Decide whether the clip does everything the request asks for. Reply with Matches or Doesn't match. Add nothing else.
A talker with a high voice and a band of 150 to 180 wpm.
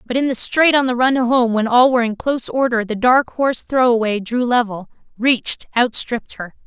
Doesn't match